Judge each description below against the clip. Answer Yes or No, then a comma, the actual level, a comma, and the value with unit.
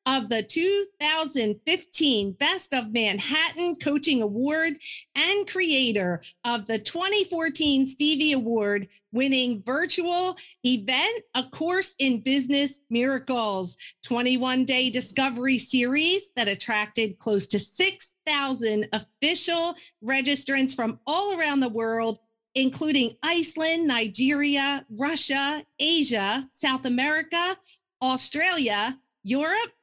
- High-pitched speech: Yes, very high, 270 Hz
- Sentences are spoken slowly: Yes, slow, 95 wpm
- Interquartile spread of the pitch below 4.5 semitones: No, average, 5.2 semitones